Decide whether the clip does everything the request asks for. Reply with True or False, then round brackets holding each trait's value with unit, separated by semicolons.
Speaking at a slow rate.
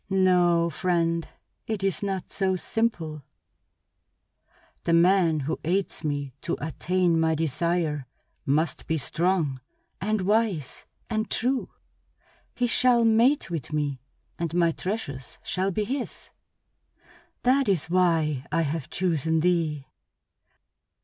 True (115 wpm)